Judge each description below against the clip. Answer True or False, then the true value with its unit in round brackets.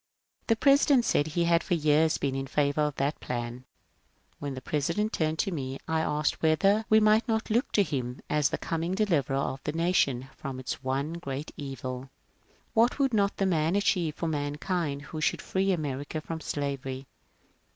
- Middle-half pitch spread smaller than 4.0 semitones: False (5.1 semitones)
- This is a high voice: False (155 Hz)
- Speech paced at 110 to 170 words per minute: False (180 wpm)